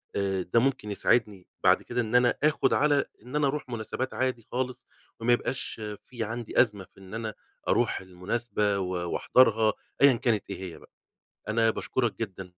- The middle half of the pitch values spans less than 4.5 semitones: Yes, average, 3.7 semitones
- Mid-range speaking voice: No, low, 115 Hz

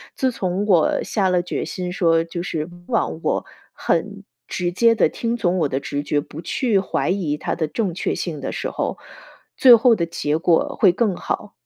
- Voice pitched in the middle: Yes, medium, 180 Hz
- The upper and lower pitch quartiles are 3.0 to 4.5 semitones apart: Yes, average, 4.1 semitones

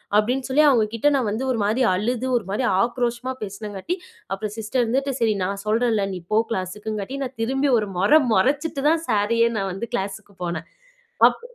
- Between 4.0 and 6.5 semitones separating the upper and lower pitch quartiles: Yes, average, 4.3 semitones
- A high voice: Yes, high, 225 Hz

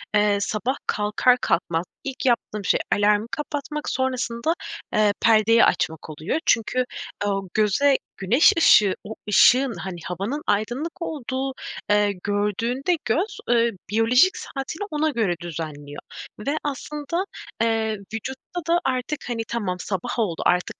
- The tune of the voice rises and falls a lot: No, average, 5.0 semitones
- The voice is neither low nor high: No, high, 230 Hz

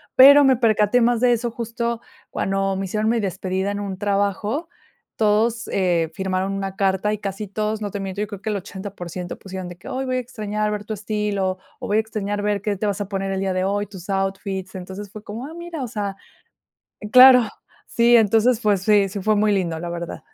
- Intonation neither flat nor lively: No, narrow, 2.3 semitones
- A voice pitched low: No, high, 205 Hz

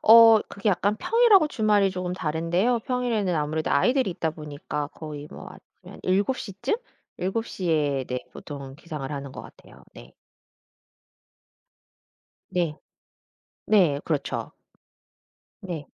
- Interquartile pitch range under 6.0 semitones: No, wide, 6.3 semitones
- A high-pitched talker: No, medium, 180 Hz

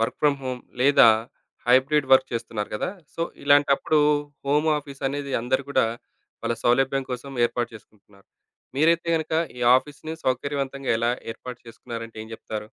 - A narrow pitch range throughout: No, average, 3.3 semitones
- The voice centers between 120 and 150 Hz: Yes, low, 135 Hz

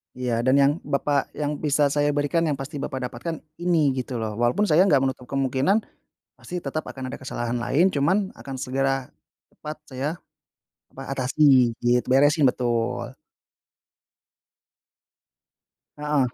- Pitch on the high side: No, low, 135 Hz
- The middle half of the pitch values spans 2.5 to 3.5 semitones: Yes, average, 2.8 semitones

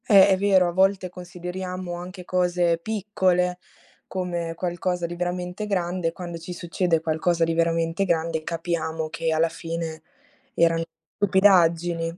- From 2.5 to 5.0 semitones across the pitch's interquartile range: No, narrow, 1.7 semitones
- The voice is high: No, medium, 175 Hz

